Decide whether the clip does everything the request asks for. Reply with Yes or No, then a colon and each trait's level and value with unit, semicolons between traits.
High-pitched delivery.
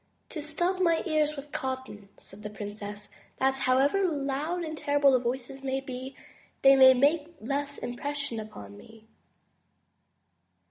Yes: very high, 270 Hz